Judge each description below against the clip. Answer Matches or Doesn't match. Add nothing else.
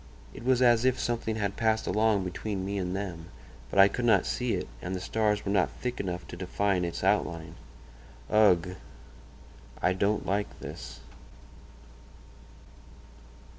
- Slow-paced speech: Doesn't match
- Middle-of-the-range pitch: Doesn't match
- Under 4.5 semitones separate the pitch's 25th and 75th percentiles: Matches